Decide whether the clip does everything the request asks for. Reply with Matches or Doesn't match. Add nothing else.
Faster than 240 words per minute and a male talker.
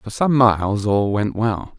Doesn't match